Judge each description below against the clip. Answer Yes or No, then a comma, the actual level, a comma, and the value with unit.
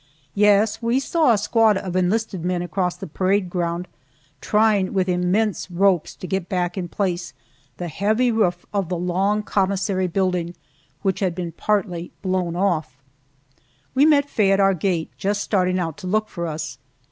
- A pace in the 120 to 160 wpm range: No, average, 170 wpm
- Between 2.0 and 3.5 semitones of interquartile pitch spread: Yes, average, 2.7 semitones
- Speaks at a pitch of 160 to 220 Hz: Yes, high, 190 Hz